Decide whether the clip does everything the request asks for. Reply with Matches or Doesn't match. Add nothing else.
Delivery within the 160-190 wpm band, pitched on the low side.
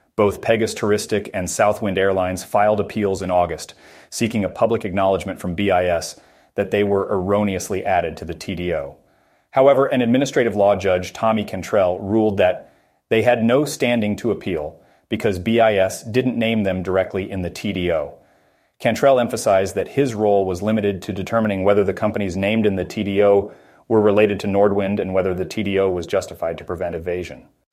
Matches